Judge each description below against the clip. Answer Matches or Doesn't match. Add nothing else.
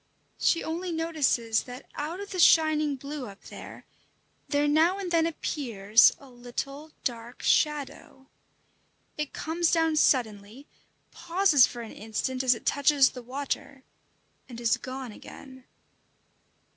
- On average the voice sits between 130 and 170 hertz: Doesn't match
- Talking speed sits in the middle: Doesn't match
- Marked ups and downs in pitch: Doesn't match